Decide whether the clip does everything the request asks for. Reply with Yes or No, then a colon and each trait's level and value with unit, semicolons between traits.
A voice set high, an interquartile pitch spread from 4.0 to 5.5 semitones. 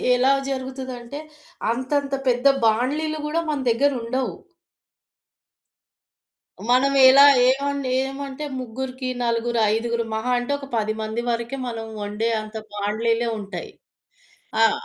No: very high, 250 Hz; average, 3.0 semitones